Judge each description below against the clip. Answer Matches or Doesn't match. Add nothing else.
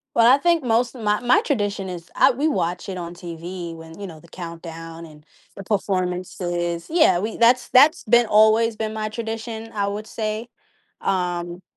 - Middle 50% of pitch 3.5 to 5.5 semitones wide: Matches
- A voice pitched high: Matches